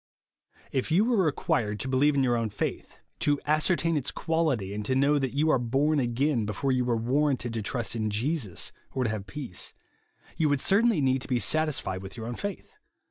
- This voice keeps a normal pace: No, fast, 210 wpm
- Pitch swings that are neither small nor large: Yes, average, 4.6 semitones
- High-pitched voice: No, low, 135 Hz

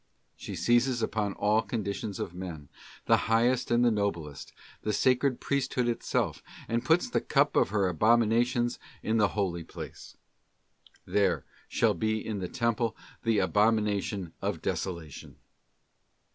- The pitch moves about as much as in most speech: Yes, average, 3.3 semitones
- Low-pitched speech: Yes, low, 110 Hz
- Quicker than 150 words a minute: No, average, 140 wpm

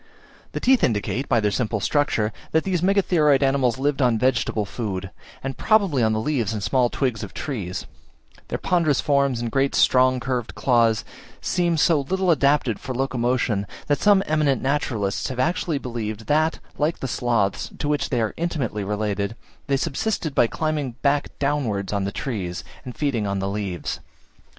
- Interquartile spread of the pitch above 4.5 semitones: Yes, average, 5.2 semitones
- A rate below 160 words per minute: No, average, 170 wpm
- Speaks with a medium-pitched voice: No, low, 130 Hz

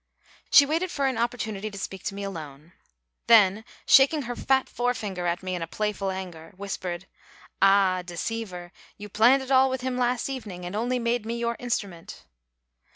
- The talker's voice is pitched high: Yes, high, 210 Hz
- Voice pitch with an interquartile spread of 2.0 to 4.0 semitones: No, average, 4.9 semitones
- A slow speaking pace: No, average, 170 wpm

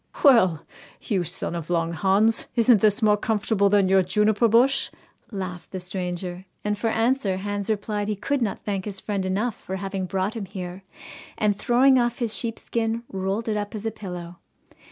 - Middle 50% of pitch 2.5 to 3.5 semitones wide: Yes, average, 3.0 semitones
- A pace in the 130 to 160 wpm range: No, average, 180 wpm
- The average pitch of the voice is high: Yes, high, 205 Hz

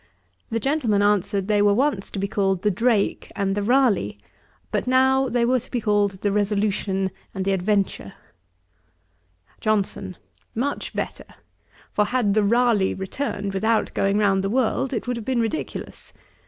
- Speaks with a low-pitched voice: No, high, 210 Hz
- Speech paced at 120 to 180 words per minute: Yes, average, 160 wpm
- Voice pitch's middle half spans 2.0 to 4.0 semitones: Yes, average, 3.5 semitones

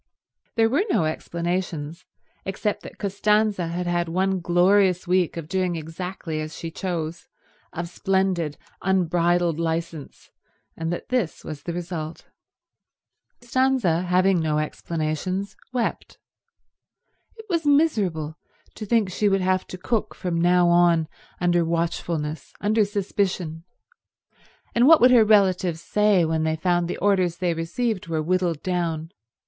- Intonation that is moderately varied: Yes, average, 3.0 semitones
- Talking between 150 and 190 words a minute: No, slow, 135 wpm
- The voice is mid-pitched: Yes, medium, 175 Hz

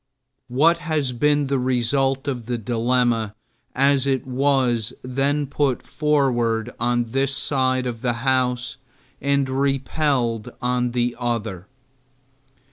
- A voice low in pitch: Yes, low, 130 Hz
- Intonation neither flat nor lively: No, narrow, 2.3 semitones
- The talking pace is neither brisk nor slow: No, slow, 120 wpm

